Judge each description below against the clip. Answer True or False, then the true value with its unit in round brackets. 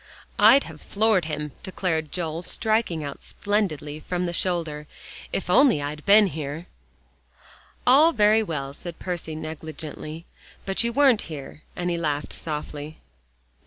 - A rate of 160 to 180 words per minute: False (140 wpm)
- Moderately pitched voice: True (165 Hz)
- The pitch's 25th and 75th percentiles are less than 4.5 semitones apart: False (5.0 semitones)